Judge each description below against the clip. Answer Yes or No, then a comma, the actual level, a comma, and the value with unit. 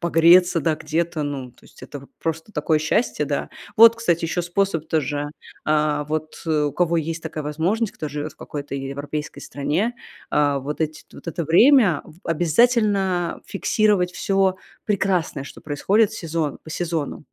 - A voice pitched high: No, medium, 160 Hz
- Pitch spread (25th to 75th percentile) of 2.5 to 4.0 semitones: Yes, average, 3.6 semitones